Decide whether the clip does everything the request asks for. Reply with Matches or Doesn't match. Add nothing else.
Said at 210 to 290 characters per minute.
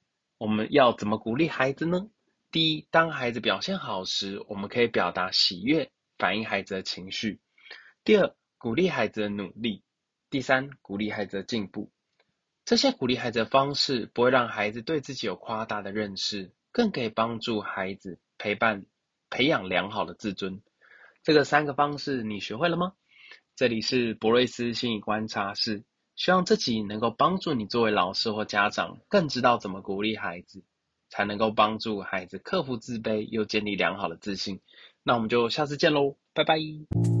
Matches